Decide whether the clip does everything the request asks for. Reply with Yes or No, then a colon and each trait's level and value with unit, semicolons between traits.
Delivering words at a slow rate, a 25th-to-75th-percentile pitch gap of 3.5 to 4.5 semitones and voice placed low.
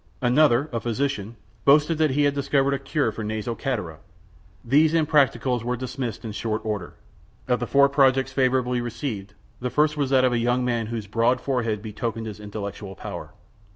No: average, 180 wpm; average, 3.8 semitones; low, 125 Hz